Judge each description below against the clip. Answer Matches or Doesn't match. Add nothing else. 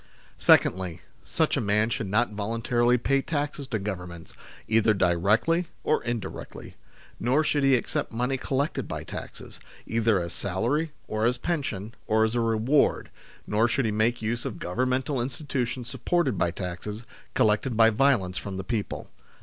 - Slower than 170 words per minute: Matches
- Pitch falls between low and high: Doesn't match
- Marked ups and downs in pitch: Doesn't match